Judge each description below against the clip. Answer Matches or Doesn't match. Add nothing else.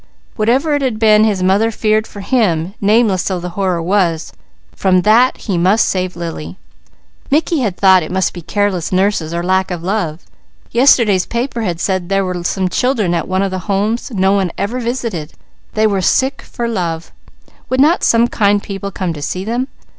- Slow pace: Doesn't match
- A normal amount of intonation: Matches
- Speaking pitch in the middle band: Doesn't match